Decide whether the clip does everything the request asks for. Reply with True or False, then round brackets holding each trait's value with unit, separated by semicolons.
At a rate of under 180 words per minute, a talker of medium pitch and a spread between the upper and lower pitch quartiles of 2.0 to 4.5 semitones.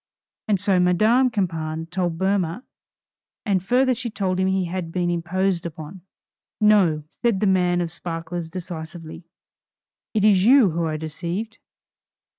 True (140 wpm; 180 Hz; 3.3 semitones)